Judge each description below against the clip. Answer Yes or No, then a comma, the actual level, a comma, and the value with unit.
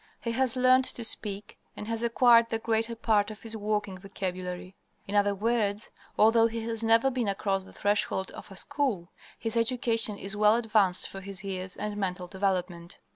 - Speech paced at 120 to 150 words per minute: No, average, 180 wpm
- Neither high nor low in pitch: No, high, 210 Hz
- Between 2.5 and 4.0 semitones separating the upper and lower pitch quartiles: Yes, average, 2.9 semitones